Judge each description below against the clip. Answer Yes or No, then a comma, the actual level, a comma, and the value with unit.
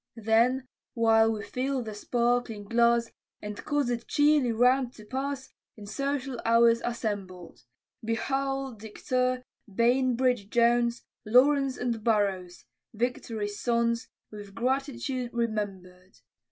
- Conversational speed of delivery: No, slow, 115 wpm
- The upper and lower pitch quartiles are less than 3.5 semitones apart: Yes, average, 2.9 semitones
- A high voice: Yes, high, 235 Hz